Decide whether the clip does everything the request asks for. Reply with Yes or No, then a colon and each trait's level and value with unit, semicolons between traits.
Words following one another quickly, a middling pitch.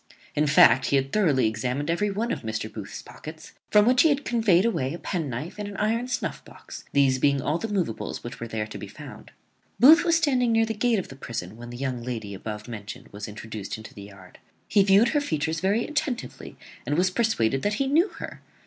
Yes: fast, 220 wpm; medium, 155 Hz